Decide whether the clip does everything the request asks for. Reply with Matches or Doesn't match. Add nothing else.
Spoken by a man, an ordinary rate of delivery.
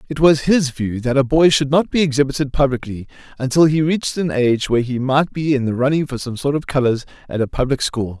Doesn't match